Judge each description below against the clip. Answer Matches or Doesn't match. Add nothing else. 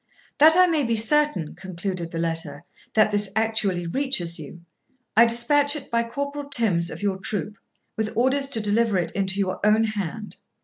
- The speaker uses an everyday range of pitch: Doesn't match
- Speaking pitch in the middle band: Doesn't match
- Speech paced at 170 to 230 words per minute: Matches